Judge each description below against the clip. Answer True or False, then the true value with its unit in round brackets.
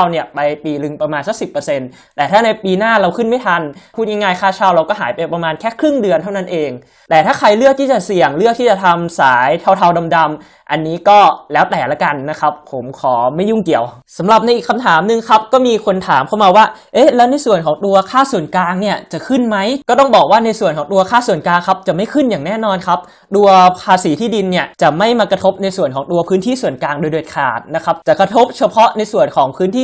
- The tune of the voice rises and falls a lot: True (5.7 semitones)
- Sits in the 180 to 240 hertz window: True (190 Hz)